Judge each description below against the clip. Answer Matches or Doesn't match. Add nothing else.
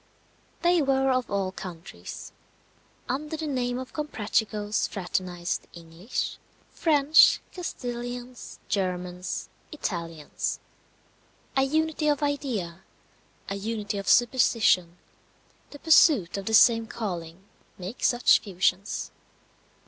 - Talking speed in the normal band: Doesn't match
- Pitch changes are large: Matches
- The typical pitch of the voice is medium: Doesn't match